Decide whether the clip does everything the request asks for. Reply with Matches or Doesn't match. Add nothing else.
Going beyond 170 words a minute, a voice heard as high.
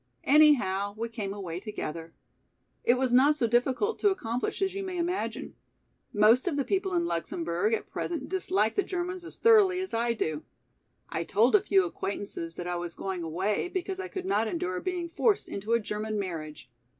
Matches